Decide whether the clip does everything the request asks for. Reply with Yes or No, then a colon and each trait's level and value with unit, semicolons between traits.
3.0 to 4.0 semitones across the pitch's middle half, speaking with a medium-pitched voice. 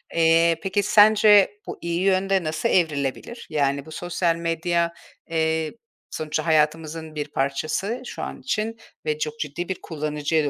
Yes: average, 3.4 semitones; medium, 165 Hz